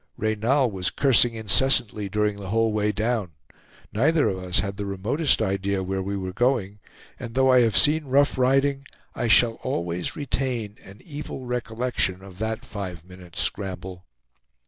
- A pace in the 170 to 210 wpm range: No, average, 160 wpm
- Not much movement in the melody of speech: No, average, 4.8 semitones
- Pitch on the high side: No, low, 110 Hz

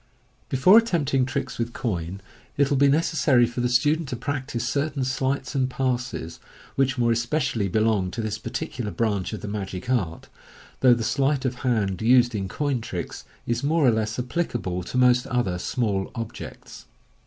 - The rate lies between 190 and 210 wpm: No, average, 175 wpm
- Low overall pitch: Yes, low, 125 Hz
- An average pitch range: Yes, average, 3.8 semitones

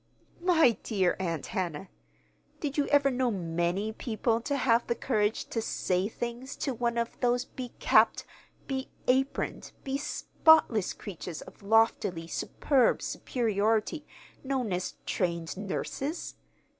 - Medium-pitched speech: No, high, 230 Hz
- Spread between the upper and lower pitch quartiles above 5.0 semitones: Yes, wide, 5.4 semitones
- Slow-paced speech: Yes, slow, 120 wpm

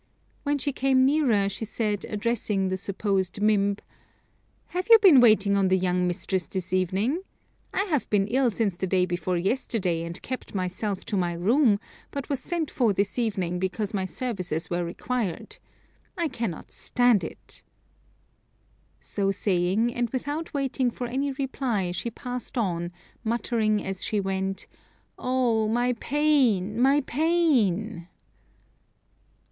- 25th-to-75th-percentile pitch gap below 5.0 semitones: No, average, 5.3 semitones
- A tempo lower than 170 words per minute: Yes, average, 140 wpm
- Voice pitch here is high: Yes, high, 215 Hz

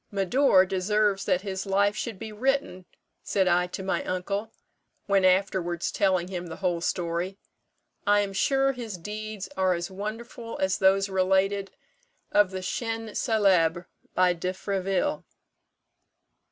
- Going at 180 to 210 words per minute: No, average, 140 wpm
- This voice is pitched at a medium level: No, high, 195 Hz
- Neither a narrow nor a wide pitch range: No, narrow, 2.2 semitones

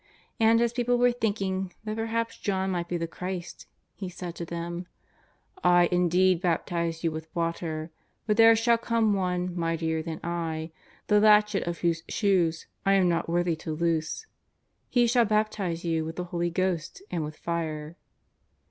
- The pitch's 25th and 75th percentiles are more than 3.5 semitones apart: Yes, average, 4.0 semitones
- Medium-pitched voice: Yes, medium, 180 Hz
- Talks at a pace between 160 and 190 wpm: Yes, average, 170 wpm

